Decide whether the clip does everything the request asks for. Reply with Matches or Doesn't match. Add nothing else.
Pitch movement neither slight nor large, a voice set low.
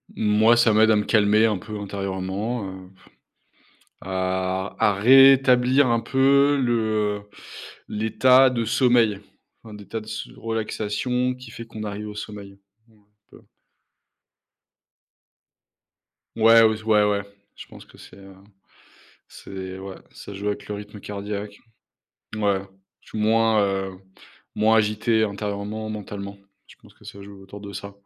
Doesn't match